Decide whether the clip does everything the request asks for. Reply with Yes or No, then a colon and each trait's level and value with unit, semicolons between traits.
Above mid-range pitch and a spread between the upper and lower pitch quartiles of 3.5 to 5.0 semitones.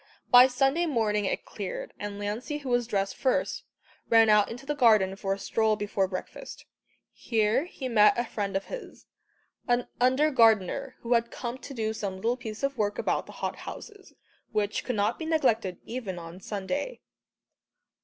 Yes: high, 230 Hz; average, 4.2 semitones